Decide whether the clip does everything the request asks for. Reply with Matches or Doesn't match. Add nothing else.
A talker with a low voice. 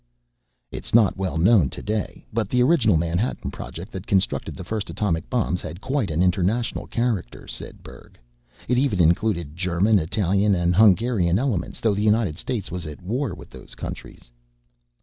Matches